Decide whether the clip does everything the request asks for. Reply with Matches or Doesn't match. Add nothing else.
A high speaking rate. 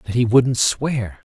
Doesn't match